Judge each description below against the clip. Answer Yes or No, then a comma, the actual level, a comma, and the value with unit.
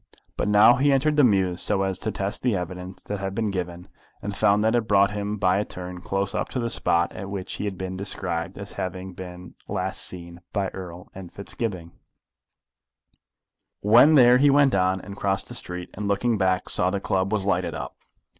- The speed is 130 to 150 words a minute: No, fast, 205 wpm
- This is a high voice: No, very low, 95 Hz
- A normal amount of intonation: No, narrow, 2.3 semitones